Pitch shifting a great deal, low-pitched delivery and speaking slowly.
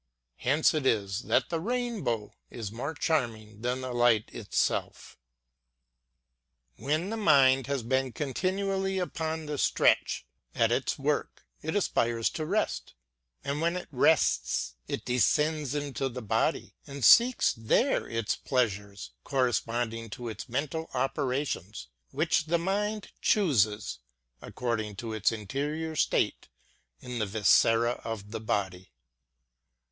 Yes: wide, 6.0 semitones; low, 130 Hz; slow, 130 wpm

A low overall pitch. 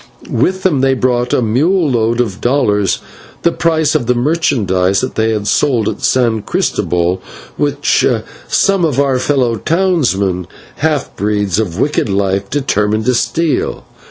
Yes: low, 125 Hz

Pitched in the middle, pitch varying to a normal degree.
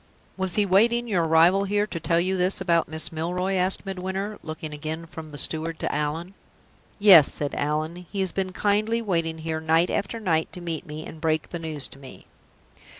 Yes: medium, 170 Hz; average, 3.3 semitones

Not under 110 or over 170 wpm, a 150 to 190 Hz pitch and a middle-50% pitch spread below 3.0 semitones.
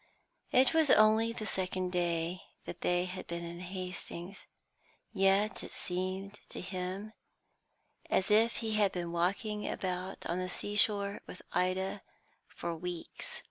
Yes: average, 140 wpm; medium, 185 Hz; narrow, 2.6 semitones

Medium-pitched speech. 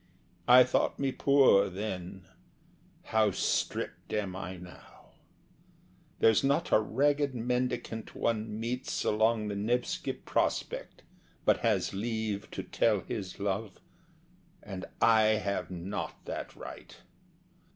No: low, 110 Hz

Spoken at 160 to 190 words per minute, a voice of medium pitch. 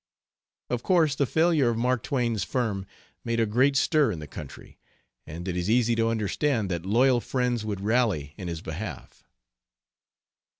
No: average, 165 wpm; low, 115 Hz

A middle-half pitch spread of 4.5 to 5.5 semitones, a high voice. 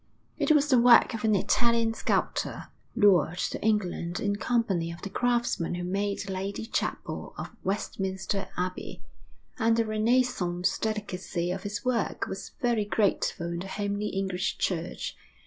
No: average, 3.6 semitones; high, 205 Hz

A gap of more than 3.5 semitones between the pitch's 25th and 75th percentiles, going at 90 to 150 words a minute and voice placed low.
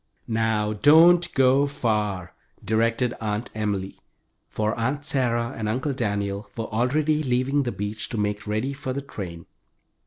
Yes: average, 4.3 semitones; average, 145 wpm; low, 115 Hz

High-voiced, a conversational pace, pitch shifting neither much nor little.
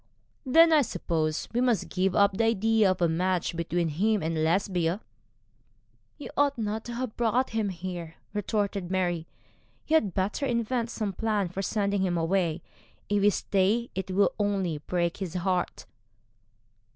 Yes: high, 195 Hz; average, 165 wpm; average, 4.0 semitones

